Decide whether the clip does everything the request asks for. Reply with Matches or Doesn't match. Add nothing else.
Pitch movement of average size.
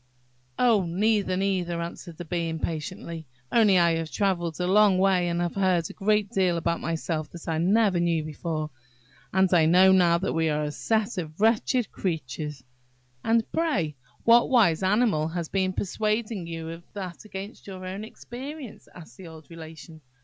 Matches